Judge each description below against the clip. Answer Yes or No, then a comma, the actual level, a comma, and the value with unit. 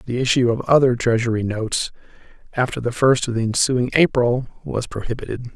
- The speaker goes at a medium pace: Yes, average, 160 wpm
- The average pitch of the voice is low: Yes, low, 120 Hz